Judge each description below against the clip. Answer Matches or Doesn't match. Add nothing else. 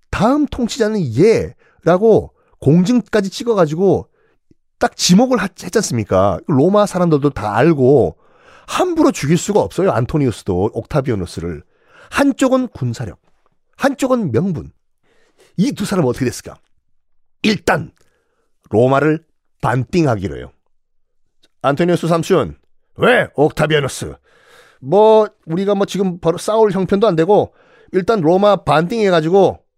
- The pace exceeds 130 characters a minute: Matches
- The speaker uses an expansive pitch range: Matches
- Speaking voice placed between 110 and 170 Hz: Doesn't match